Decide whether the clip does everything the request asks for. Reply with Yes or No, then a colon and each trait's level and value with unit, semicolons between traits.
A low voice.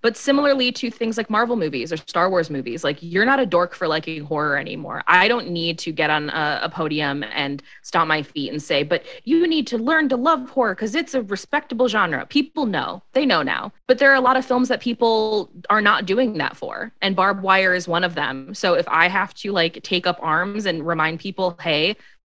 No: high, 195 Hz